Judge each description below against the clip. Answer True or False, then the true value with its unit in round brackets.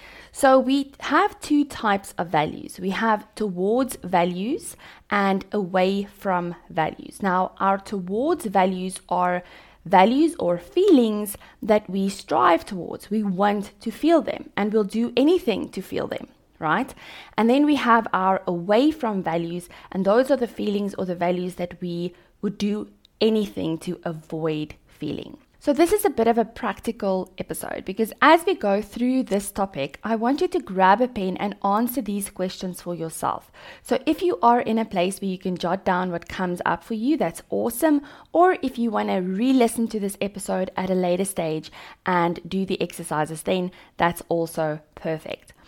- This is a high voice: True (200 Hz)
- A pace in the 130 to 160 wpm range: False (175 wpm)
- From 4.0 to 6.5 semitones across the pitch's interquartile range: True (4.8 semitones)